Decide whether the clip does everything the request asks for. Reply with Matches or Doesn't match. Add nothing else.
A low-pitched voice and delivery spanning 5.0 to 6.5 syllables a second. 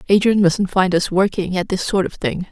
Doesn't match